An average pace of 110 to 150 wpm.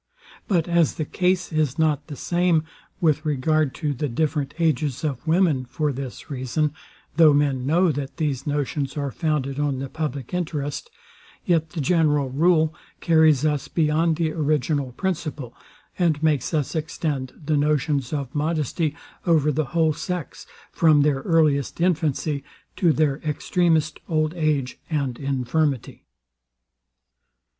Yes: average, 140 wpm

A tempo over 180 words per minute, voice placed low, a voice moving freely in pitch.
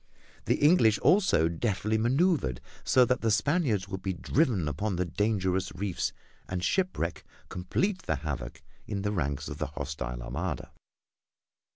No: average, 140 wpm; very low, 95 Hz; wide, 6.7 semitones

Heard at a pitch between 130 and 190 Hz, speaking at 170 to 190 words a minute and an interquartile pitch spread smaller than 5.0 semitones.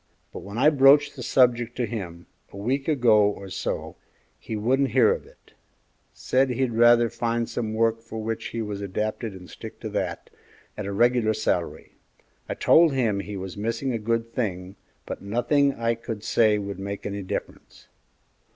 No: low, 115 Hz; average, 180 wpm; average, 3.1 semitones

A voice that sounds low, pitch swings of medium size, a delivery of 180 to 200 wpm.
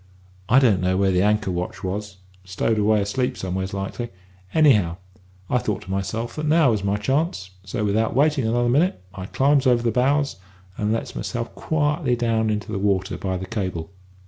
Yes: low, 110 Hz; average, 4.6 semitones; average, 185 wpm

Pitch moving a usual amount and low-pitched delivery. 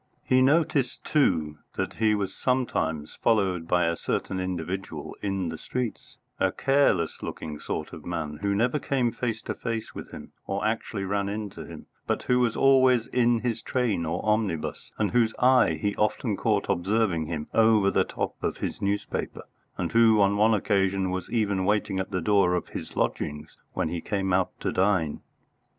Yes: average, 3.8 semitones; low, 100 Hz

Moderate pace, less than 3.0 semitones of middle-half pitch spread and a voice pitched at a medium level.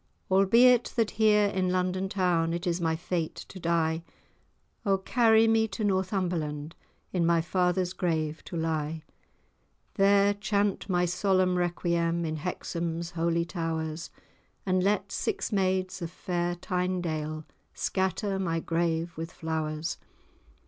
No: slow, 130 wpm; narrow, 2.6 semitones; medium, 180 Hz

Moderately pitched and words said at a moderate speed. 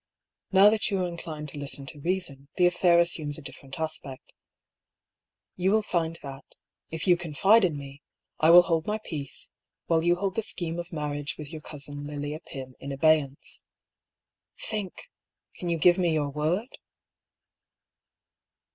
Yes: medium, 160 Hz; average, 165 wpm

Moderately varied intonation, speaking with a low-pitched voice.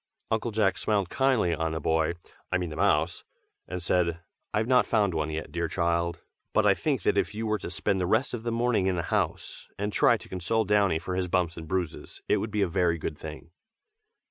Yes: average, 4.1 semitones; very low, 90 Hz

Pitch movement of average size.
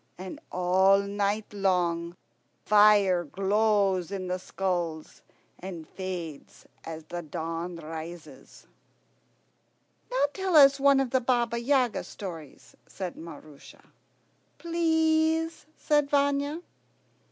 No: wide, 7.7 semitones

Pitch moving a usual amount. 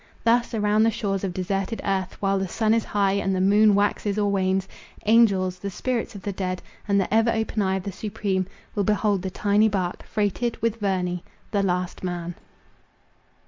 No: narrow, 2.2 semitones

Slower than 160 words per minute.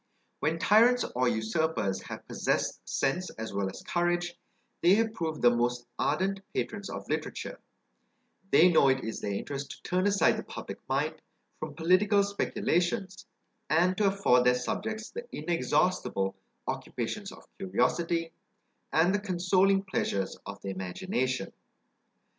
Yes: average, 140 wpm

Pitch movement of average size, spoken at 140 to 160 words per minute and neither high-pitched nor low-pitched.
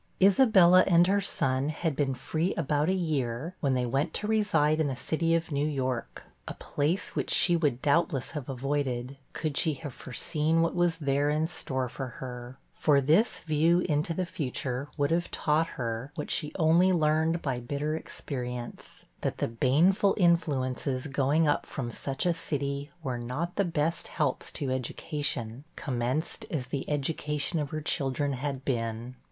No: average, 3.9 semitones; average, 170 wpm; medium, 145 Hz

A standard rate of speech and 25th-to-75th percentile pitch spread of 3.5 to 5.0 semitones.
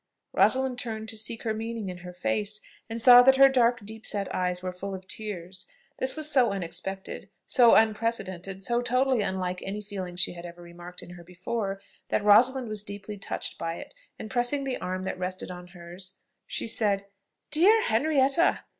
Yes: average, 185 wpm; average, 4.7 semitones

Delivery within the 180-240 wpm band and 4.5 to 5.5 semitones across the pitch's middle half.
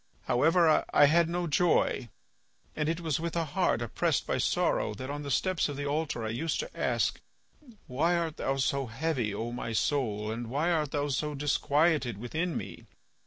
Yes: average, 185 wpm; average, 4.8 semitones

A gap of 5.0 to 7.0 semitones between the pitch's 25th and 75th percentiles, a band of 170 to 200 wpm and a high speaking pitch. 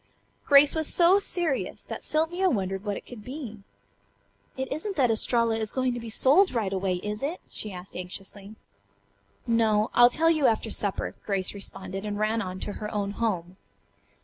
Yes: wide, 5.5 semitones; average, 175 wpm; high, 220 Hz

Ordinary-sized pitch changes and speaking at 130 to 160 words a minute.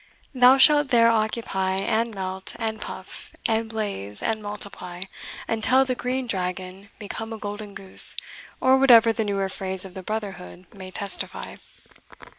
Yes: average, 3.2 semitones; average, 145 wpm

